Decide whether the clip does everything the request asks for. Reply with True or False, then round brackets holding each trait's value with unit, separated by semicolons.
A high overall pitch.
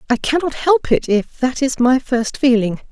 True (255 Hz)